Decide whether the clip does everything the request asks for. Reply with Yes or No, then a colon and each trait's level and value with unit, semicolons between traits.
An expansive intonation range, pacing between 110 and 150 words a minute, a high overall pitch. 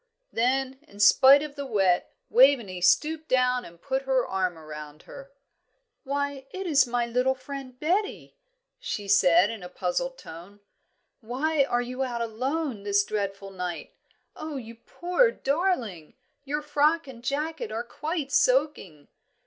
Yes: wide, 6.0 semitones; average, 145 wpm; very high, 255 Hz